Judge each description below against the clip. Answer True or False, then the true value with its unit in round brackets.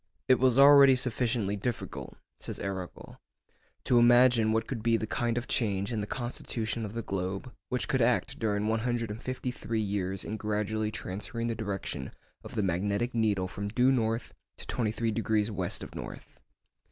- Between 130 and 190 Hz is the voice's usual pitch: False (110 Hz)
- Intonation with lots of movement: False (2.8 semitones)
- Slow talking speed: False (175 wpm)